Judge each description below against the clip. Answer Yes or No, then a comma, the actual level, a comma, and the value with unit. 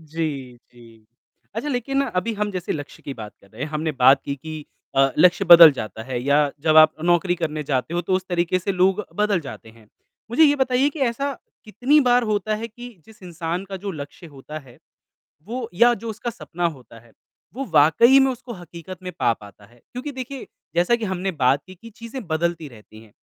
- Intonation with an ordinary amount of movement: No, wide, 7.9 semitones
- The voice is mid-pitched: Yes, medium, 175 Hz